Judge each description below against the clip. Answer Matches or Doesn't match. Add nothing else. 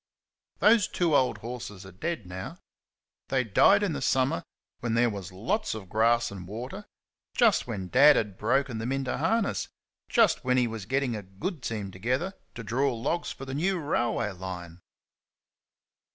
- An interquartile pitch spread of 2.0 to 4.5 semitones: Doesn't match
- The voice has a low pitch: Matches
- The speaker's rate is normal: Matches